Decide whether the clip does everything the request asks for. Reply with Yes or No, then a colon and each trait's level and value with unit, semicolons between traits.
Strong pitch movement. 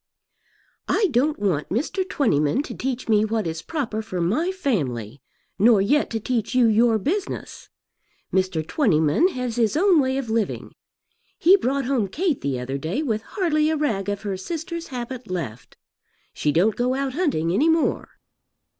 Yes: wide, 7.7 semitones